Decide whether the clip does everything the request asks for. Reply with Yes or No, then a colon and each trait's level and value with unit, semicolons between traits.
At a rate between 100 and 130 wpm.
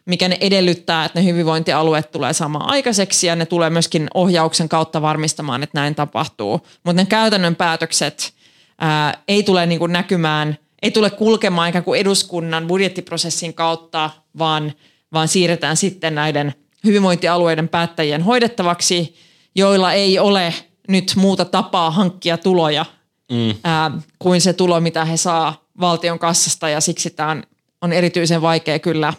No: average, 140 wpm